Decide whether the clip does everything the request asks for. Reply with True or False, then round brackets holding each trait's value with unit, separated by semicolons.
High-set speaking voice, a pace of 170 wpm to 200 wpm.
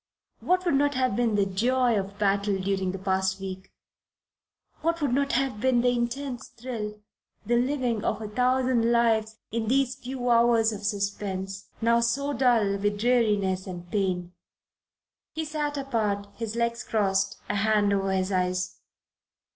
False (225 Hz; 155 wpm)